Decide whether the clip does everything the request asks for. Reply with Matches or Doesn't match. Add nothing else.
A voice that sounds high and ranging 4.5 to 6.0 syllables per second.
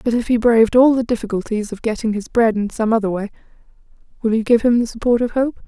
Doesn't match